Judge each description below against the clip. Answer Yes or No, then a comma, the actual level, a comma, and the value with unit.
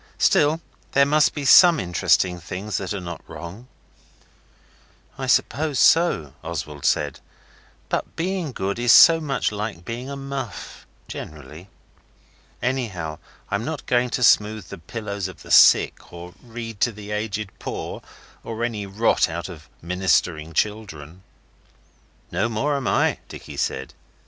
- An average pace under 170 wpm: Yes, average, 140 wpm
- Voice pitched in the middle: No, low, 105 Hz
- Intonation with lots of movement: Yes, wide, 6.2 semitones